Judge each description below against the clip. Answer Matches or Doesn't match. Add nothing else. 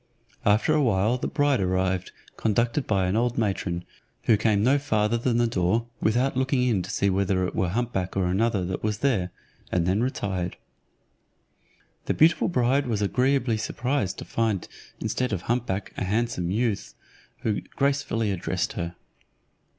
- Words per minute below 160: Doesn't match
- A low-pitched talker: Matches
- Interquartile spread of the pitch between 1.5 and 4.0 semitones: Doesn't match